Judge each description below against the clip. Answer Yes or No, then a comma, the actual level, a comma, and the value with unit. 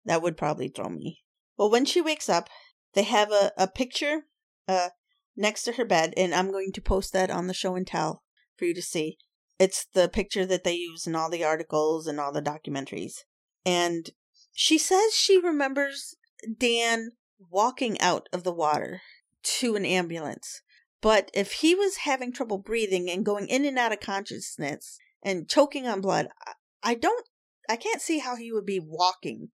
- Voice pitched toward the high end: Yes, high, 205 Hz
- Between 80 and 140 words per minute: No, average, 185 wpm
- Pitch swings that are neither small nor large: No, wide, 7.0 semitones